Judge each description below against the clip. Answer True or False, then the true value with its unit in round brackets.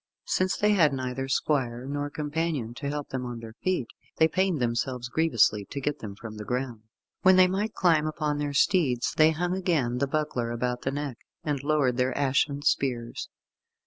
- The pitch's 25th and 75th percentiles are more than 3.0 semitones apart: True (4.3 semitones)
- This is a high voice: False (140 Hz)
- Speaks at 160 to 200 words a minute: True (185 wpm)